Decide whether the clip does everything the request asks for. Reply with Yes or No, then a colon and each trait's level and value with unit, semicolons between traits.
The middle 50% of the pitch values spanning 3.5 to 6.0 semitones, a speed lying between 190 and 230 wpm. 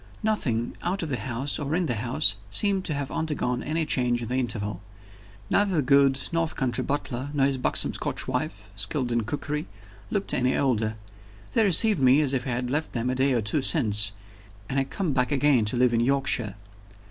Yes: average, 3.8 semitones; fast, 205 wpm